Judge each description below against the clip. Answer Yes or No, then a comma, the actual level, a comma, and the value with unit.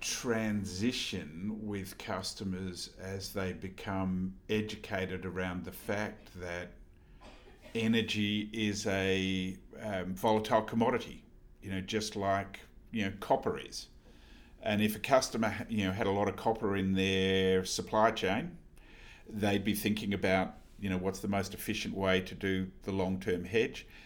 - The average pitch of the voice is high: No, low, 100 Hz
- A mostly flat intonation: Yes, narrow, 2.3 semitones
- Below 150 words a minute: Yes, average, 140 wpm